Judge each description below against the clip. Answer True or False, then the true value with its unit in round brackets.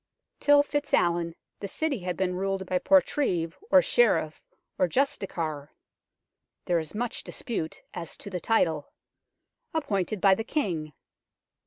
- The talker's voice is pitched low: False (190 Hz)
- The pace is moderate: False (130 wpm)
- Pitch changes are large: True (7.4 semitones)